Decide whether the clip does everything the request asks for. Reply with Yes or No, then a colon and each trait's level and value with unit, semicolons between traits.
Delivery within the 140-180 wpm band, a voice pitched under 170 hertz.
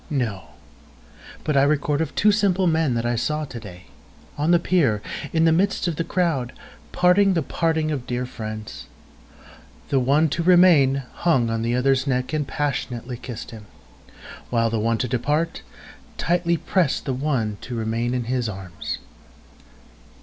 Yes: average, 150 wpm; low, 135 Hz